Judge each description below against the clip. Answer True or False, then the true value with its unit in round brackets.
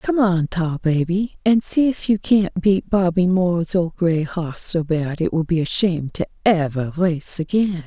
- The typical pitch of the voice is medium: True (175 Hz)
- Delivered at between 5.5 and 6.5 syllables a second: False (4.4 syllables/s)